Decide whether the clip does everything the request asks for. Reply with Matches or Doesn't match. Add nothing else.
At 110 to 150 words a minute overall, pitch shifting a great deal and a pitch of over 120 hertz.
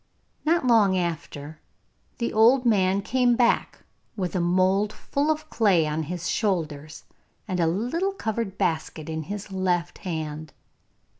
Matches